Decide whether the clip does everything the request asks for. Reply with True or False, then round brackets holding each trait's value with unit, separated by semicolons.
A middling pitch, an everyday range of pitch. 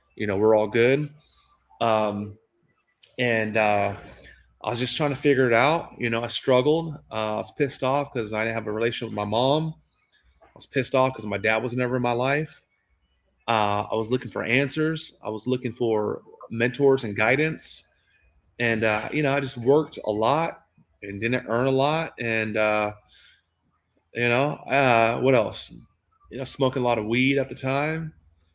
False (120 Hz; 3.8 semitones)